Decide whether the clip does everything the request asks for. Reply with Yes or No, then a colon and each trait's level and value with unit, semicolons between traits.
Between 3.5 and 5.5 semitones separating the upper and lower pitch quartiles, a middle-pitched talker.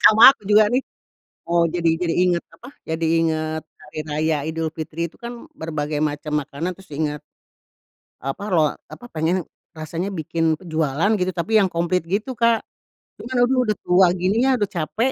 Yes: average, 4.6 semitones; medium, 170 Hz